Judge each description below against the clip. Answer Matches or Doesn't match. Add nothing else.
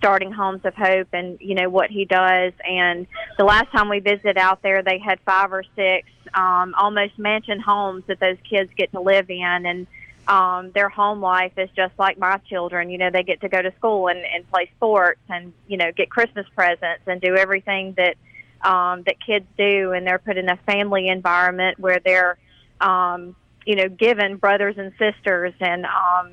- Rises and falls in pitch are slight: Matches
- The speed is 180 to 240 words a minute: Matches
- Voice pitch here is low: Doesn't match